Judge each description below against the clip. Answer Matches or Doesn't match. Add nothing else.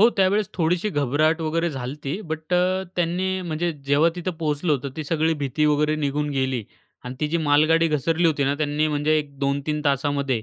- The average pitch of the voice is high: Doesn't match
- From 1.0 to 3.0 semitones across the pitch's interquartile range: Matches